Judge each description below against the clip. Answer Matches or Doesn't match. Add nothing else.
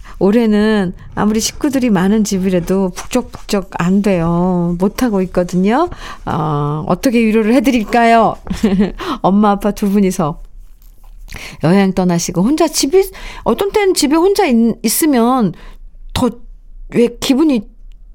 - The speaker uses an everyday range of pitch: Matches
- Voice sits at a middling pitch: Doesn't match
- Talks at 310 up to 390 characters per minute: Doesn't match